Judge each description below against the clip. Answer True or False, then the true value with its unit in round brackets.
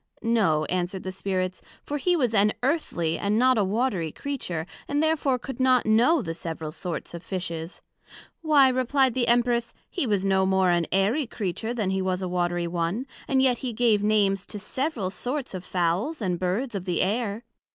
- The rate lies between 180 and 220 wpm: True (195 wpm)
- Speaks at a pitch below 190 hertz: False (205 Hz)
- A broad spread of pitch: True (5.8 semitones)